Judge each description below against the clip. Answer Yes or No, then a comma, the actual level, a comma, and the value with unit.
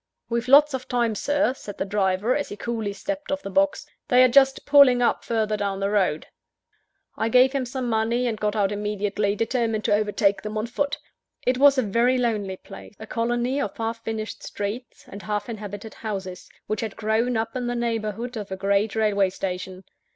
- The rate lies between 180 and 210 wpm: Yes, average, 200 wpm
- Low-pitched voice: No, high, 220 Hz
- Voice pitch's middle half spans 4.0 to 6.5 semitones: No, average, 3.3 semitones